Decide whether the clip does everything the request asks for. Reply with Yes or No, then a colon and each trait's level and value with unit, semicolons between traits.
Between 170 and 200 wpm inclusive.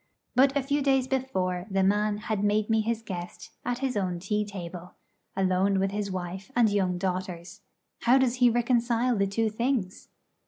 Yes: average, 180 wpm